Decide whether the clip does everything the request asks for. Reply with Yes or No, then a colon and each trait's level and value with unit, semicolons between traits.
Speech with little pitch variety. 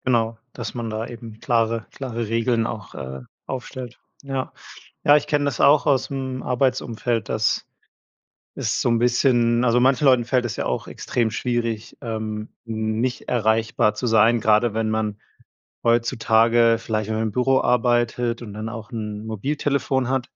Yes: narrow, 2.2 semitones